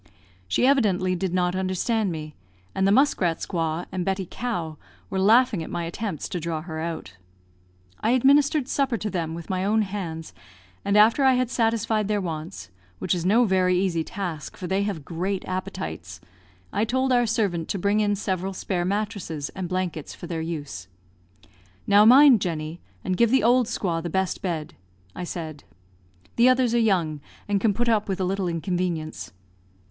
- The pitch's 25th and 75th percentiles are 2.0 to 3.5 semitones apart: No, average, 4.4 semitones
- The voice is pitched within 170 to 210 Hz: Yes, high, 190 Hz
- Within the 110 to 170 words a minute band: No, average, 180 wpm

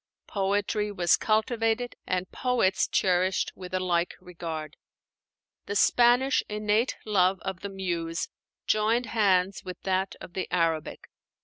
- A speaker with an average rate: No, slow, 125 wpm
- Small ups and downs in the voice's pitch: No, average, 3.1 semitones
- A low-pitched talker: No, high, 190 Hz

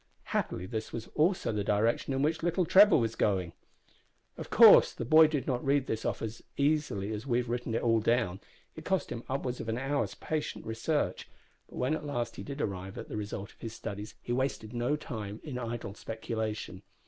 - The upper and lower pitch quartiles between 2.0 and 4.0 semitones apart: No, average, 4.7 semitones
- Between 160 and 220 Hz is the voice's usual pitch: No, low, 120 Hz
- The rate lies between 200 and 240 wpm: Yes, fast, 205 wpm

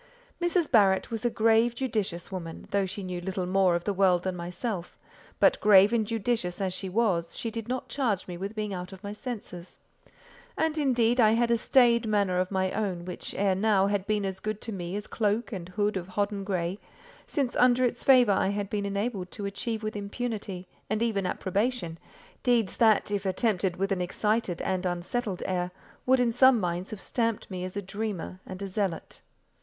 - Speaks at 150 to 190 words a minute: No, average, 200 wpm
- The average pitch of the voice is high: Yes, high, 200 Hz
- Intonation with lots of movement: No, average, 3.5 semitones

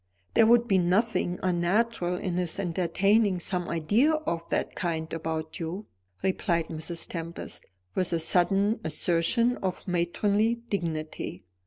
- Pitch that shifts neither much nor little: Yes, average, 3.6 semitones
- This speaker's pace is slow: Yes, slow, 130 wpm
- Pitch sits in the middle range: Yes, medium, 180 Hz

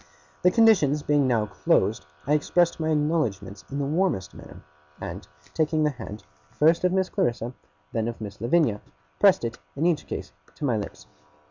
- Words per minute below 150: No, average, 175 wpm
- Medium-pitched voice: Yes, medium, 145 Hz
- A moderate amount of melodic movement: No, wide, 6.6 semitones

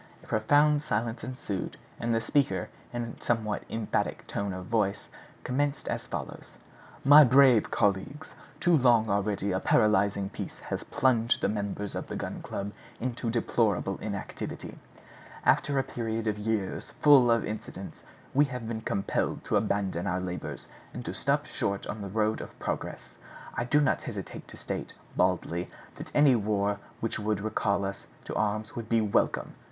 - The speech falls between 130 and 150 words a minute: No, average, 165 wpm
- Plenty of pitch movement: No, average, 3.3 semitones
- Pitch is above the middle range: No, low, 110 Hz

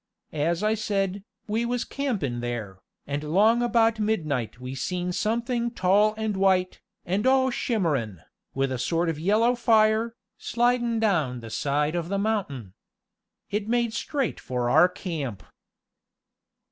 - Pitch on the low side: No, high, 195 Hz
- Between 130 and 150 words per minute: Yes, average, 140 wpm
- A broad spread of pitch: Yes, wide, 7.5 semitones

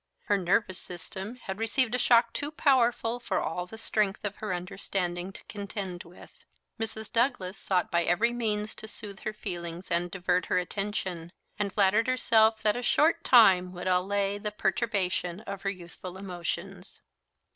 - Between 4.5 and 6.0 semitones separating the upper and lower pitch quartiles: No, average, 3.6 semitones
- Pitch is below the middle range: No, high, 200 Hz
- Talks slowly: No, average, 165 wpm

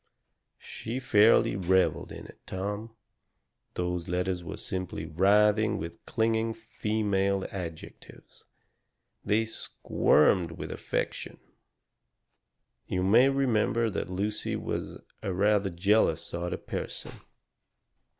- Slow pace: Yes, slow, 105 wpm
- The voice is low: Yes, low, 100 Hz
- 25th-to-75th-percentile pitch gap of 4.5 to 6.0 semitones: No, average, 3.5 semitones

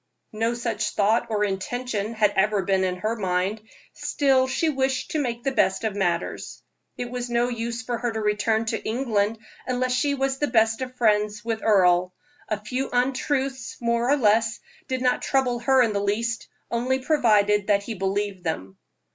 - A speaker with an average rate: Yes, average, 180 wpm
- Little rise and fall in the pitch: No, average, 3.3 semitones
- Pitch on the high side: Yes, high, 230 Hz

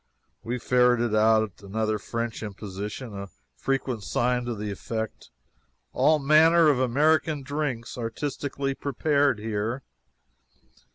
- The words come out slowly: Yes, slow, 110 wpm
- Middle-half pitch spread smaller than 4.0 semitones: No, average, 4.3 semitones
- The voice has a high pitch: No, low, 120 Hz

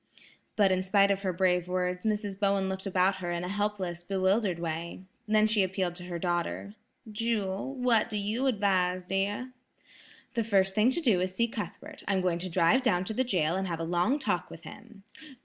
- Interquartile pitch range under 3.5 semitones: Yes, average, 2.7 semitones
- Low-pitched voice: No, high, 190 Hz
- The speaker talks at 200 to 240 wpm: Yes, fast, 205 wpm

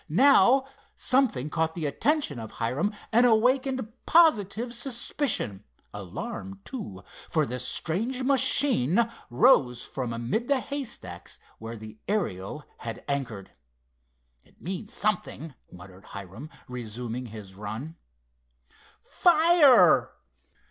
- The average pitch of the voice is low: No, medium, 160 Hz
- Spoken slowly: Yes, slow, 105 wpm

